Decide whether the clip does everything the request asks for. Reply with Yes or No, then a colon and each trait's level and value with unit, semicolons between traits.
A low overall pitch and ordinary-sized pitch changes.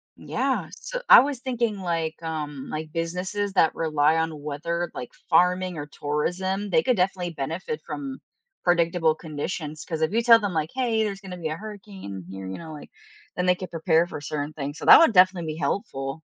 No: medium, 170 Hz; average, 4.0 semitones